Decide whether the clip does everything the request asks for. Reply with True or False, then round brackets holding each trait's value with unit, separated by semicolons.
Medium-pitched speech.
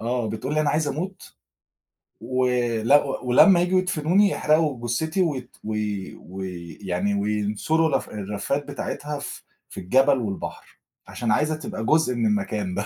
False (125 Hz)